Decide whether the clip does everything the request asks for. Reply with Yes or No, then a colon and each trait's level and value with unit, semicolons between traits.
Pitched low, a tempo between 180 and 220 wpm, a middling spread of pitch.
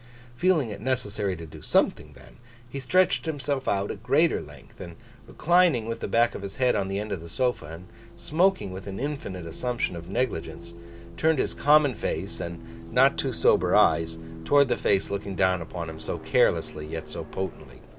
No: low, 105 Hz; average, 190 wpm; wide, 7.7 semitones